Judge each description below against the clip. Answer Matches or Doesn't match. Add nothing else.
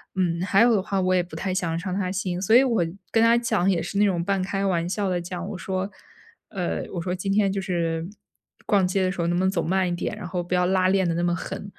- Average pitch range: Doesn't match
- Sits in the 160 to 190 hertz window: Matches